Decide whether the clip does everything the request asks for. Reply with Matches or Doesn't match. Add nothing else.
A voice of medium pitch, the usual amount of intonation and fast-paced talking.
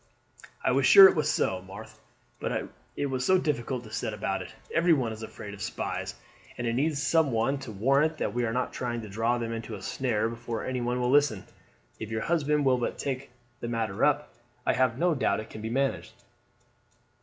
Doesn't match